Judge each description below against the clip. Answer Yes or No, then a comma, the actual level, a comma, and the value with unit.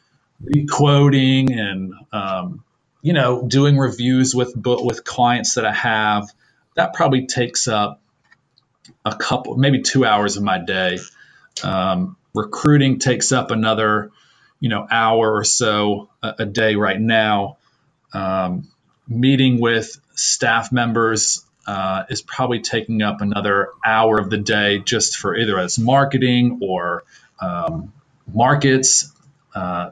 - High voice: No, low, 120 Hz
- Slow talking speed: Yes, slow, 130 wpm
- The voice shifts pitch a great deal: No, average, 3.9 semitones